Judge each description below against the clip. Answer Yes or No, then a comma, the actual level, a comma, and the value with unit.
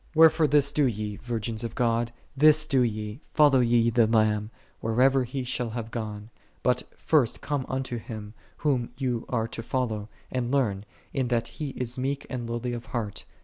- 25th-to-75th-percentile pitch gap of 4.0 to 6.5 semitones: No, average, 2.9 semitones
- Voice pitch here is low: Yes, low, 120 Hz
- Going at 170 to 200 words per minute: Yes, average, 185 wpm